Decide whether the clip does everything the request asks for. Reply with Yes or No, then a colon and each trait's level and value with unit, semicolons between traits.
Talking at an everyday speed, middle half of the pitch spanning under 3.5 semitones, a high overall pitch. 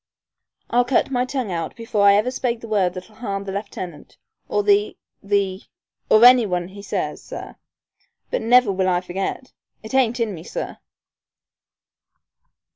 No: average, 160 wpm; average, 3.9 semitones; high, 205 Hz